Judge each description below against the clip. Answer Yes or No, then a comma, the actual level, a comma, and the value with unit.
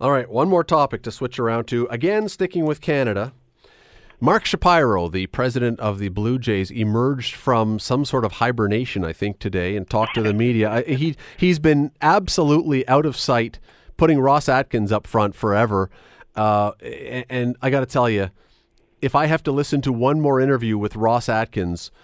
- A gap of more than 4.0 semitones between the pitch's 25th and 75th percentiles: Yes, average, 4.6 semitones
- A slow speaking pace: No, average, 185 wpm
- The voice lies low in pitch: Yes, low, 120 Hz